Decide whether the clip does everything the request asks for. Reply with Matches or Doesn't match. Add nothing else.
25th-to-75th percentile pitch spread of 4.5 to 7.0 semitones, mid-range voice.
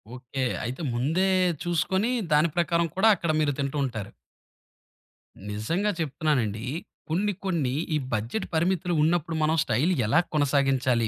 Matches